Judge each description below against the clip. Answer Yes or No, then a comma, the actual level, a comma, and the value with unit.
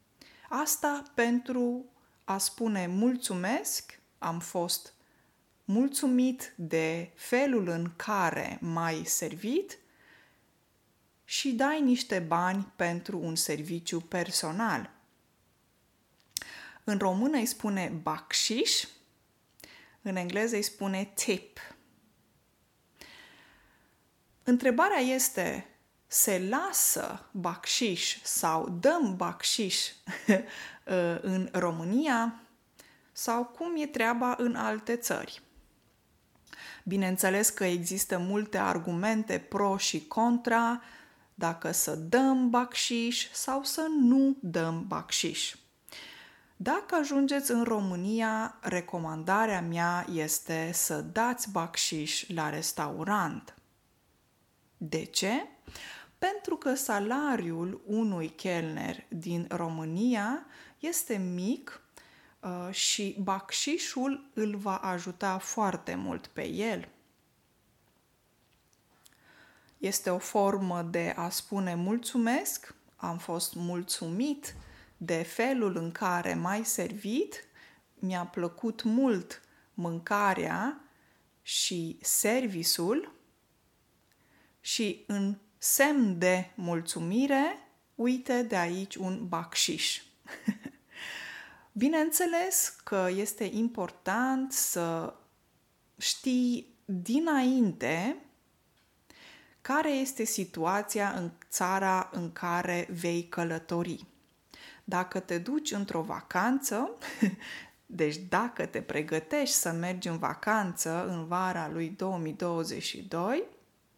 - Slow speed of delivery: Yes, slow, 85 wpm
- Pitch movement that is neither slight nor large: No, wide, 6.1 semitones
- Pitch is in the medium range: No, high, 200 Hz